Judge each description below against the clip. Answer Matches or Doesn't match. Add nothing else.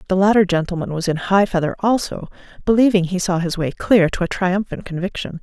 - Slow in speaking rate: Doesn't match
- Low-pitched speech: Doesn't match